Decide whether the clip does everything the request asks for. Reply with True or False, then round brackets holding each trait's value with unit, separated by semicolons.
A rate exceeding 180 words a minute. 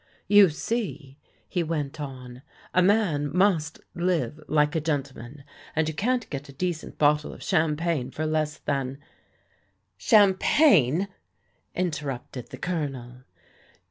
False (135 wpm)